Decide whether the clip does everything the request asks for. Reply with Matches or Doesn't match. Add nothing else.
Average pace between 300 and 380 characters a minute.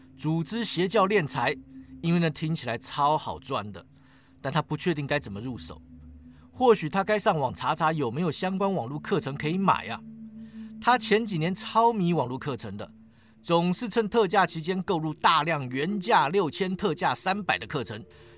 Doesn't match